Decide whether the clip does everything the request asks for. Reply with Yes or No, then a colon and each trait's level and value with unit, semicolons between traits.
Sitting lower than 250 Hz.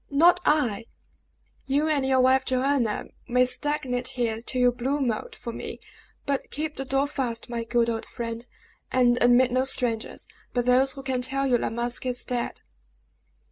No: very high, 255 Hz